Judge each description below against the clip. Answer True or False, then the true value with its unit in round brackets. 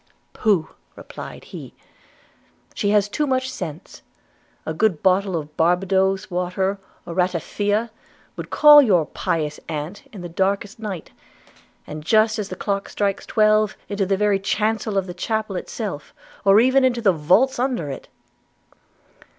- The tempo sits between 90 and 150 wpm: True (145 wpm)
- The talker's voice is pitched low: False (200 Hz)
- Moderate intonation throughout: True (3.3 semitones)